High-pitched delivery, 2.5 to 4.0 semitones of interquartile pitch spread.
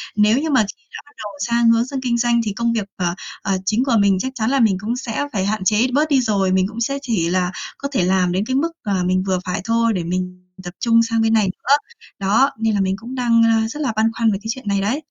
Yes: high, 225 Hz; average, 3.7 semitones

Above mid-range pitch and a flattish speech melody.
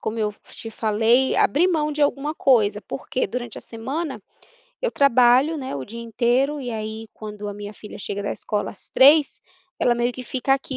No: high, 240 Hz; average, 4.1 semitones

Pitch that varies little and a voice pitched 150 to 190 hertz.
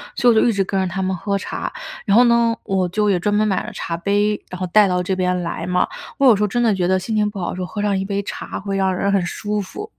No: narrow, 2.2 semitones; high, 200 Hz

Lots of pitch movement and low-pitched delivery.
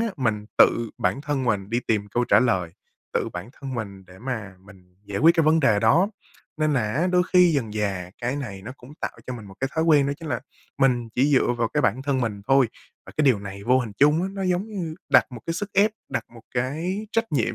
Yes: wide, 6.5 semitones; low, 125 Hz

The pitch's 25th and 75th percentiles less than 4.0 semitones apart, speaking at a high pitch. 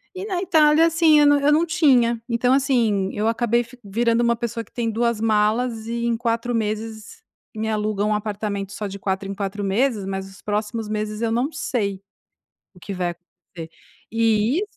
Yes: average, 2.8 semitones; high, 225 Hz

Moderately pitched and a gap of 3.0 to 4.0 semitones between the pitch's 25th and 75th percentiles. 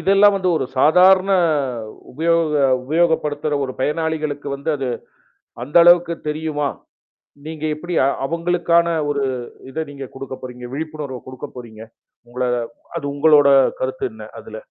Yes: medium, 155 Hz; average, 3.4 semitones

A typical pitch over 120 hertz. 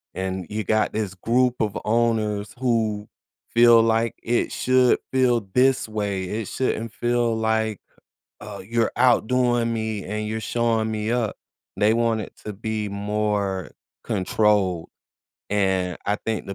No: low, 110 Hz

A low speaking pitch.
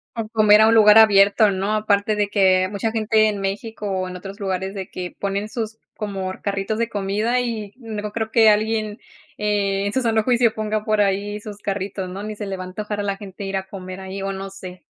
No: high, 205 Hz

